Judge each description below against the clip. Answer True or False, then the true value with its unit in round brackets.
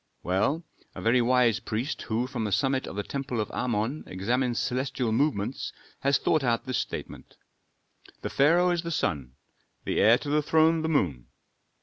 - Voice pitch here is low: True (125 Hz)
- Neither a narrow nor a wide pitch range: True (4.5 semitones)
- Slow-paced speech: False (175 wpm)